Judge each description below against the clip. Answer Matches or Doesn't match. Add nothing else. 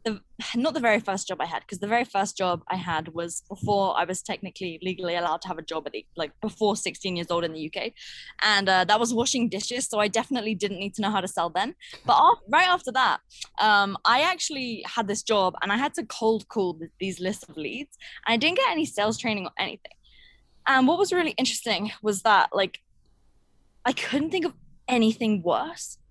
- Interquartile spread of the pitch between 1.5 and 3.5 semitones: Doesn't match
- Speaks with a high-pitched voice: Matches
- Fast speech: Matches